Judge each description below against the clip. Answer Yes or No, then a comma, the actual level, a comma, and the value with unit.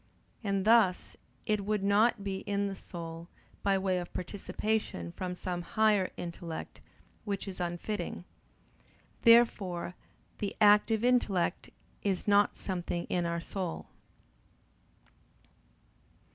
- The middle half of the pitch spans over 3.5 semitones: No, average, 2.9 semitones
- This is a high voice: Yes, high, 195 Hz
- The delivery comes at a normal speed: No, slow, 110 wpm